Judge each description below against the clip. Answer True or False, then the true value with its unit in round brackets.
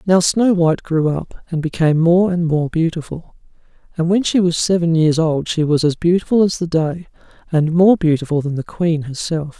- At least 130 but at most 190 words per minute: False (200 wpm)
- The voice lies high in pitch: False (165 Hz)